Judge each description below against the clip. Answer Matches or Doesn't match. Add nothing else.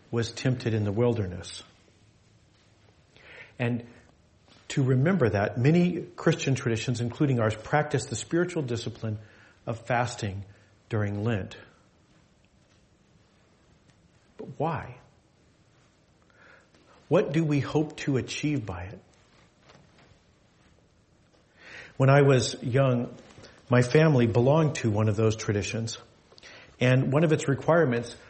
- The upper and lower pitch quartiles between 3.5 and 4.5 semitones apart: Matches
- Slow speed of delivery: Matches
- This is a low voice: Matches